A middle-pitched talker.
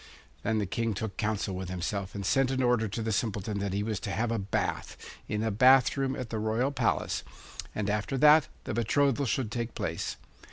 No: low, 110 Hz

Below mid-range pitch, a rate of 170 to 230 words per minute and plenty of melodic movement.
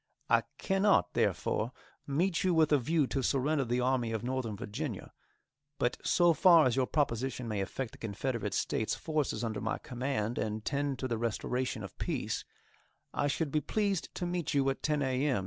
No: low, 130 Hz; average, 185 wpm; average, 4.7 semitones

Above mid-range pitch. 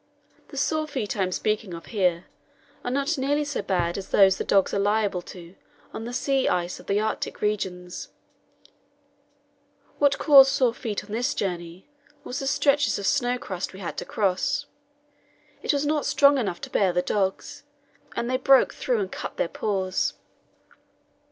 Yes: high, 215 Hz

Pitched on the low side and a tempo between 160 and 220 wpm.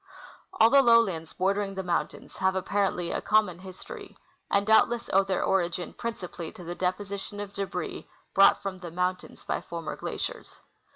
No: high, 190 Hz; average, 165 wpm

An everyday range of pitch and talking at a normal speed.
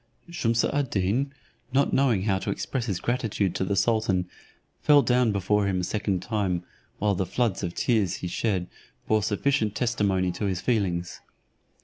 Yes: average, 4.0 semitones; average, 165 wpm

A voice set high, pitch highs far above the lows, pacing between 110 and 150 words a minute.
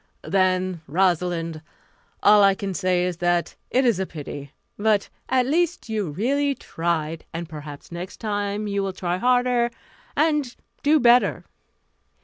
Yes: high, 195 Hz; wide, 5.7 semitones; average, 140 wpm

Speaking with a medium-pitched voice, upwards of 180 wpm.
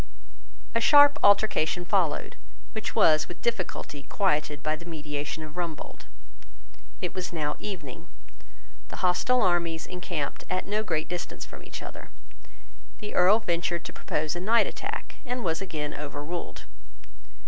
No: medium, 175 Hz; average, 140 wpm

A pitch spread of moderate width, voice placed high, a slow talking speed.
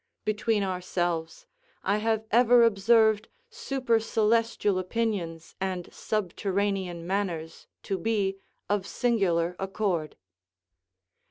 Yes: average, 3.5 semitones; high, 200 Hz; slow, 85 wpm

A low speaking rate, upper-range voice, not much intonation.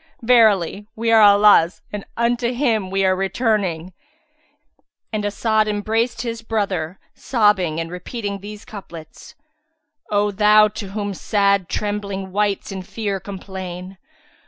Yes: slow, 130 wpm; high, 205 Hz; narrow, 2.2 semitones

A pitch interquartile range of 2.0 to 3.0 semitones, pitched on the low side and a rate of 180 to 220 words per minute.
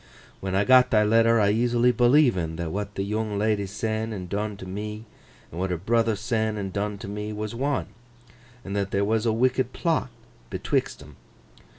Yes: narrow, 2.5 semitones; low, 105 Hz; average, 195 wpm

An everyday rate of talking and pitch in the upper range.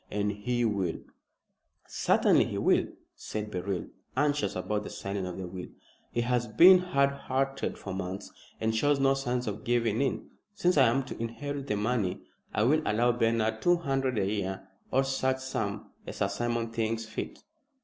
No: average, 180 wpm; low, 115 Hz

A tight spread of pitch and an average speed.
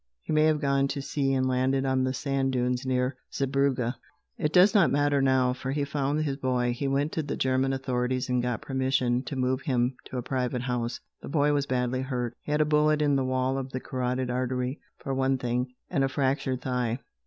No: narrow, 1.6 semitones; fast, 220 wpm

